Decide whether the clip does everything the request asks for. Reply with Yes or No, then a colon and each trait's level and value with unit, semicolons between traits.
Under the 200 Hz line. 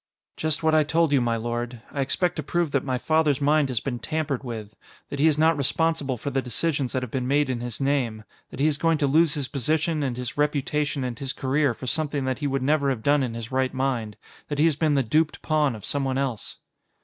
Yes: medium, 140 Hz